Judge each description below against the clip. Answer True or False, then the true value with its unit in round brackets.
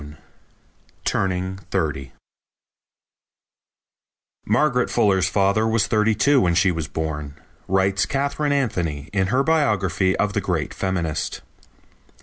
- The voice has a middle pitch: False (95 Hz)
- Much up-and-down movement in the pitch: False (4.5 semitones)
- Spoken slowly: True (115 wpm)